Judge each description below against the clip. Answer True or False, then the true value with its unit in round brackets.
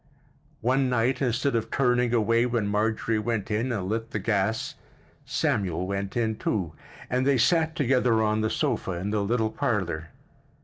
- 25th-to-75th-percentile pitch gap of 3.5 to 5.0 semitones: False (3.1 semitones)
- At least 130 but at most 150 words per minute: False (165 wpm)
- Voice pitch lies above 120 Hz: False (110 Hz)